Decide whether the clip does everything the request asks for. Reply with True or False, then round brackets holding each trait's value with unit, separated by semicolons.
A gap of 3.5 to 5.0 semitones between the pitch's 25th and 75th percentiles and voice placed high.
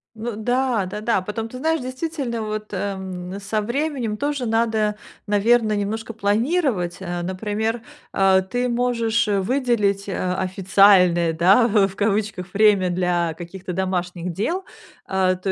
True (3.8 semitones; 210 Hz)